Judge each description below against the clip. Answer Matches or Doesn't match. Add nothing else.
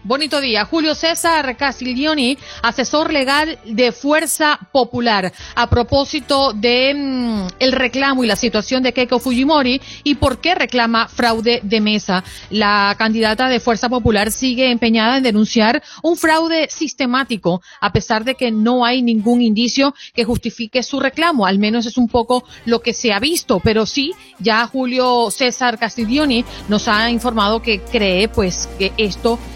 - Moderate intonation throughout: Matches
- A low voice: Doesn't match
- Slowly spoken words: Doesn't match